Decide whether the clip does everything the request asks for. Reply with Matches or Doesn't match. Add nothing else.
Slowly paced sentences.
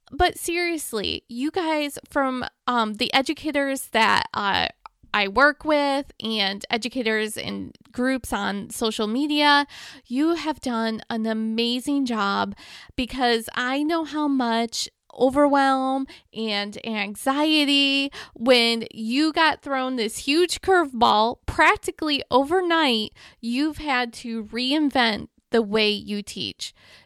Matches